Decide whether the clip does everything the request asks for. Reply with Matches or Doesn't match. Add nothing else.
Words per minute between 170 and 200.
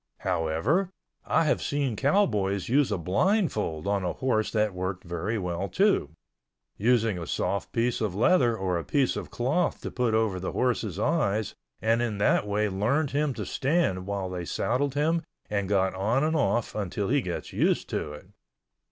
Matches